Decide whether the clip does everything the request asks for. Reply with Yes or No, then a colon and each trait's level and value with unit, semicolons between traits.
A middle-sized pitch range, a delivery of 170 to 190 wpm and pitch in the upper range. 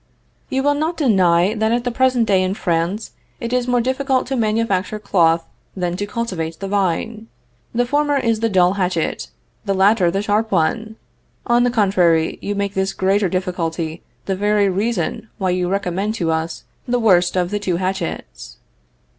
Yes: average, 4.2 semitones; average, 175 wpm; high, 200 Hz